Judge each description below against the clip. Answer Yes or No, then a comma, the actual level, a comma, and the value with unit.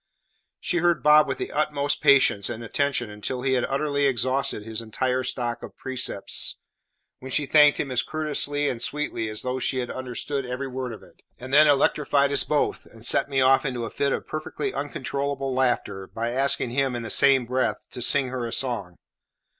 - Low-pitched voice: Yes, low, 130 Hz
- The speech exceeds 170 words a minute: Yes, average, 195 wpm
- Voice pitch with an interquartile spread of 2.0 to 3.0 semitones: Yes, narrow, 2.6 semitones